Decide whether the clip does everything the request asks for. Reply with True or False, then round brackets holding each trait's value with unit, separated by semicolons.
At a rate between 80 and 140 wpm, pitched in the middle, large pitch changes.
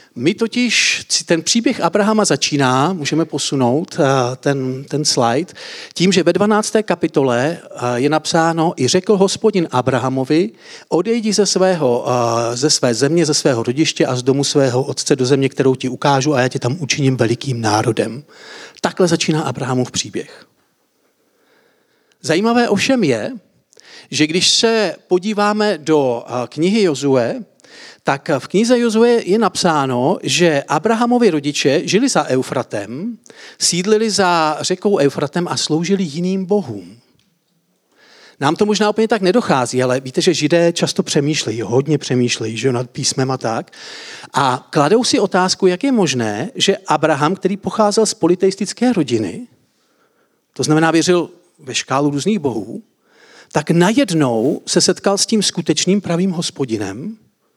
True (135 wpm; 165 Hz; 7.0 semitones)